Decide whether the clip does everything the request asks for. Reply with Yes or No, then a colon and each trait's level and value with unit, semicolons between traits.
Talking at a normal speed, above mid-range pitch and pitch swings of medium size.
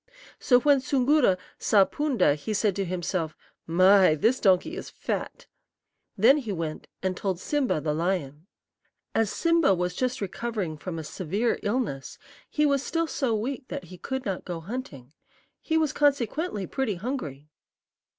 No: average, 155 wpm; high, 205 Hz; wide, 7.0 semitones